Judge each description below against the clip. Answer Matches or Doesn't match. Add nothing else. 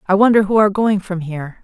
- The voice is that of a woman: Matches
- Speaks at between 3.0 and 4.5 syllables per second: Doesn't match